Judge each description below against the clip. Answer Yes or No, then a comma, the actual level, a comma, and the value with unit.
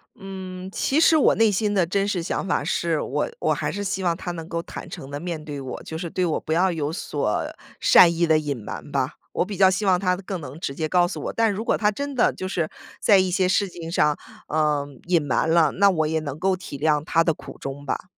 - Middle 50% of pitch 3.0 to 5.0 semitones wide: Yes, average, 3.6 semitones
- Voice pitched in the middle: Yes, medium, 175 Hz